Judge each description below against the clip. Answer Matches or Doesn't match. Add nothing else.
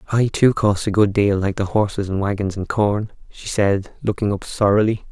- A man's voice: Matches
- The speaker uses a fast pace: Matches